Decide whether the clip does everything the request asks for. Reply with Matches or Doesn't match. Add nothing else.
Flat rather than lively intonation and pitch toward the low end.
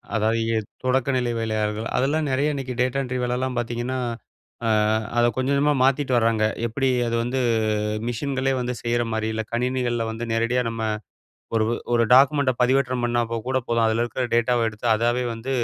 Matches